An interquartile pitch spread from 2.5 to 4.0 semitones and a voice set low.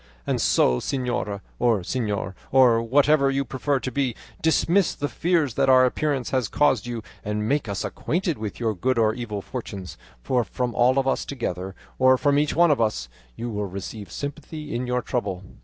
No: average, 4.4 semitones; low, 125 Hz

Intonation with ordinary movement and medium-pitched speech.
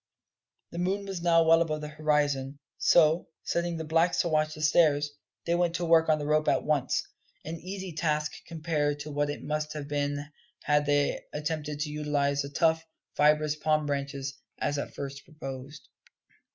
No: narrow, 2.0 semitones; medium, 150 Hz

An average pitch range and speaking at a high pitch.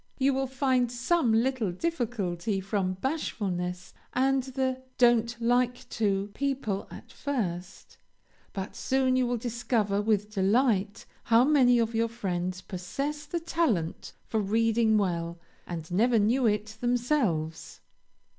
Yes: average, 4.7 semitones; high, 230 Hz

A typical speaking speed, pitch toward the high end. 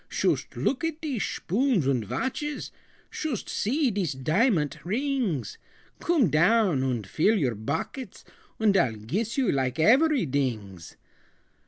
No: slow, 125 wpm; high, 195 Hz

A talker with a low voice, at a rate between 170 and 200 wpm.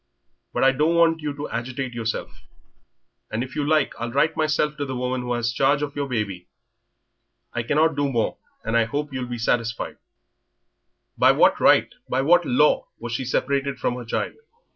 Yes: low, 130 Hz; average, 185 wpm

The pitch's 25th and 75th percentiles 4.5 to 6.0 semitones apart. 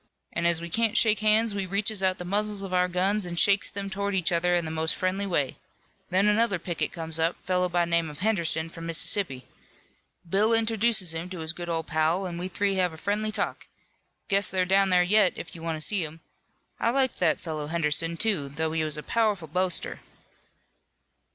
No: average, 3.5 semitones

